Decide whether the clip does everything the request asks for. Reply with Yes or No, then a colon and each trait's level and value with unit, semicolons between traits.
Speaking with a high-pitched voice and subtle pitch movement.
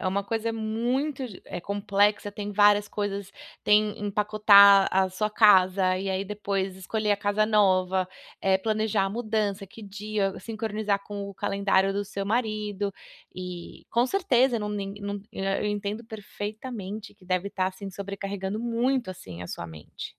Yes: high, 205 Hz; narrow, 1.7 semitones